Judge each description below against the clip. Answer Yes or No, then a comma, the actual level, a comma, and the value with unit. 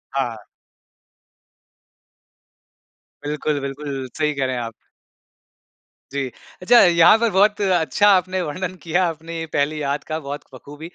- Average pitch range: Yes, average, 4.3 semitones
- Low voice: No, medium, 155 Hz